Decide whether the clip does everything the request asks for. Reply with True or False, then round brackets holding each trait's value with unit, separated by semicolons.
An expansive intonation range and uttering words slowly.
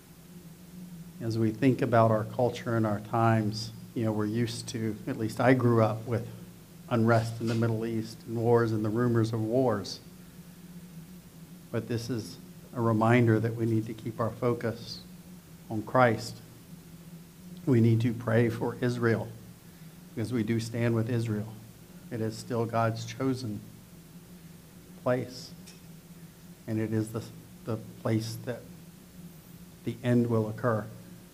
False (7.0 semitones; 145 wpm)